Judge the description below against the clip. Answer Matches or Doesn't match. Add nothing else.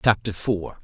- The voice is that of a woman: Doesn't match